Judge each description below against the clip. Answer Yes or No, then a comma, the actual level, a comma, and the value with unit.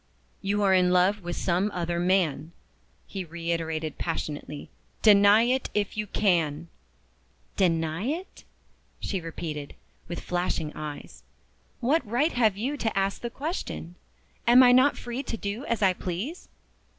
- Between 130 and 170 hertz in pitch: No, high, 190 Hz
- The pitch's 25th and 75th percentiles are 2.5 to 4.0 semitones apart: No, wide, 5.5 semitones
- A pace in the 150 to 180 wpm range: No, average, 140 wpm